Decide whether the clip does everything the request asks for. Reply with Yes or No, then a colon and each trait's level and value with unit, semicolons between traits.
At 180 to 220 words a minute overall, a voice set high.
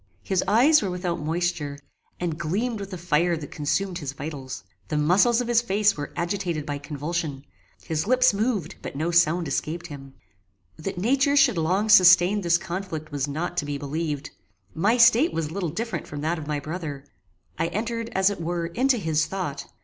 No: average, 185 wpm; medium, 175 Hz